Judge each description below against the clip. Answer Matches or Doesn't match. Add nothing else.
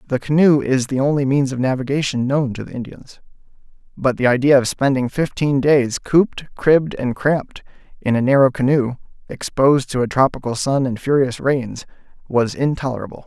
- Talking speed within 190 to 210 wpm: Doesn't match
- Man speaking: Matches